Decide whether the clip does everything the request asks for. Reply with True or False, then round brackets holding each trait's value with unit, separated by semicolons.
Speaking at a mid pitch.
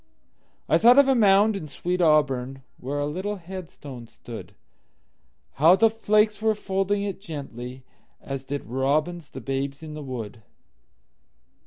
True (155 Hz)